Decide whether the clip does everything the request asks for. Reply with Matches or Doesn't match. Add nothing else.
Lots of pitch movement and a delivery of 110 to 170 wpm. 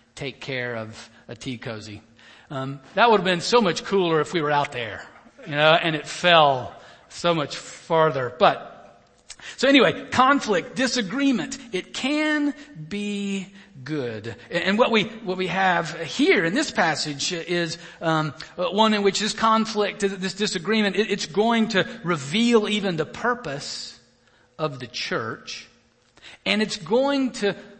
Matches